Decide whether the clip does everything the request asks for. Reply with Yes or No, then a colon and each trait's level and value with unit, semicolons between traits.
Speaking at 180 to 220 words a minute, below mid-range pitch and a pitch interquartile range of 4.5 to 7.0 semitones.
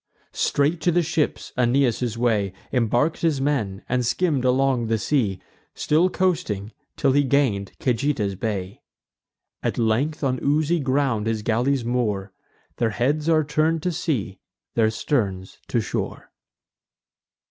No: average, 140 wpm; low, 125 Hz; average, 5.1 semitones